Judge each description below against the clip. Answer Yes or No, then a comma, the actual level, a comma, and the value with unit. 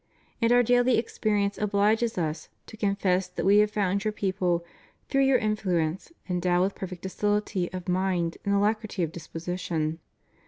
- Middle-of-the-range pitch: No, high, 195 Hz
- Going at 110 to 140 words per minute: No, average, 155 wpm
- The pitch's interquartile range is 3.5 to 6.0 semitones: No, average, 3.1 semitones